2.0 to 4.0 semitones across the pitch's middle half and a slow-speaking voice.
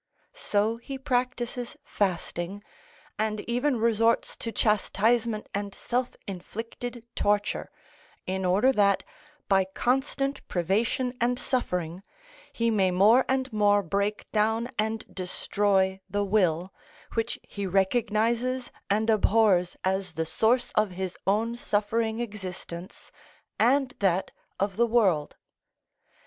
Yes: average, 3.6 semitones; slow, 115 wpm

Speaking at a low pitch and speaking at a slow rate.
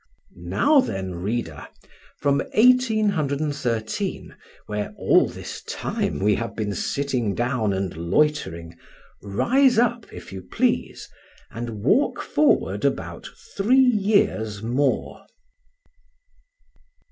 Yes: low, 125 Hz; slow, 100 wpm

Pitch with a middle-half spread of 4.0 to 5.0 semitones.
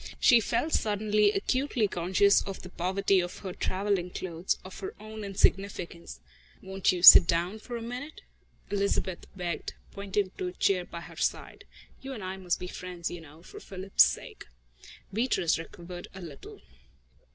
No: average, 2.7 semitones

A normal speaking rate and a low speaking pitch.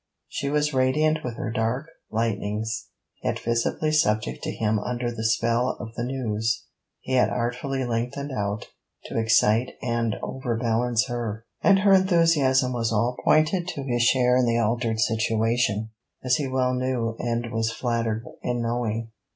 Yes: average, 155 wpm; low, 120 Hz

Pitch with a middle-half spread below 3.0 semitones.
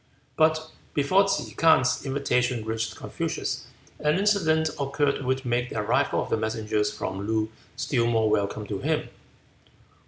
No: wide, 5.4 semitones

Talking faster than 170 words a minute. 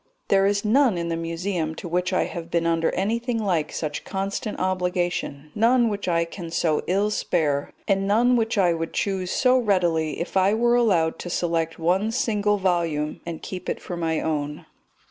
Yes: average, 185 wpm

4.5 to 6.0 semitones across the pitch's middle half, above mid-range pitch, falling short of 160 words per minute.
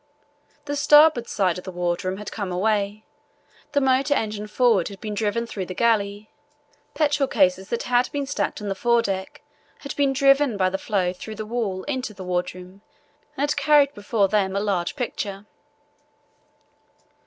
No: average, 5.3 semitones; high, 210 Hz; average, 170 wpm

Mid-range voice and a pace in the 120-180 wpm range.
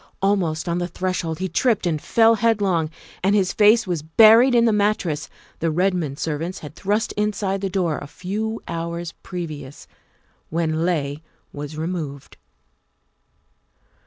Yes: medium, 180 Hz; average, 140 wpm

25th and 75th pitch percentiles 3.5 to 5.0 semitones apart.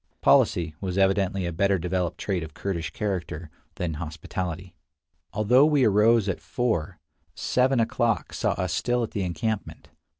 Yes: average, 4.3 semitones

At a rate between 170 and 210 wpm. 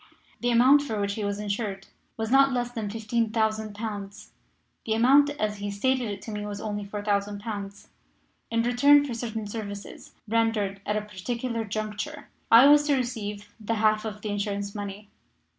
Yes: average, 175 wpm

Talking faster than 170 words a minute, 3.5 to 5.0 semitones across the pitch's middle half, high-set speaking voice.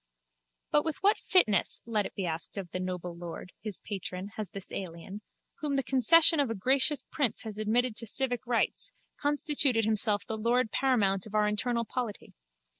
Yes: average, 180 wpm; average, 4.7 semitones; high, 220 Hz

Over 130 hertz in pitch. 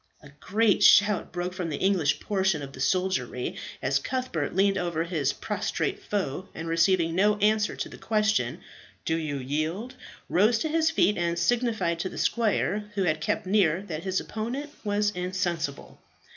Yes: medium, 185 Hz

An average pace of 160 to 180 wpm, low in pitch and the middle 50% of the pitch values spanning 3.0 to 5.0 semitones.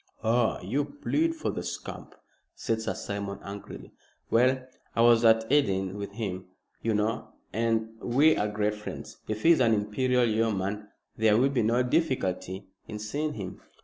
Yes: average, 165 wpm; low, 110 Hz; average, 3.4 semitones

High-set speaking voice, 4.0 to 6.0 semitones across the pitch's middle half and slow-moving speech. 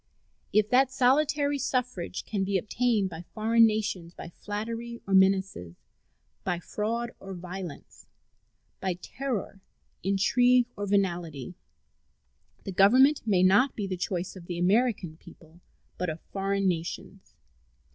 Yes: high, 195 Hz; average, 4.7 semitones; slow, 125 wpm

